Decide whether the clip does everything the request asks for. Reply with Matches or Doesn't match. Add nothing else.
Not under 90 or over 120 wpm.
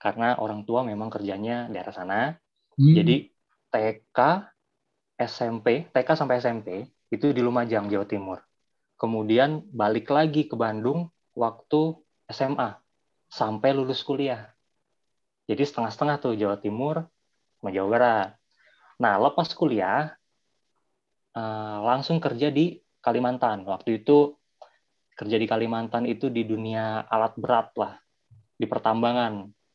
Matches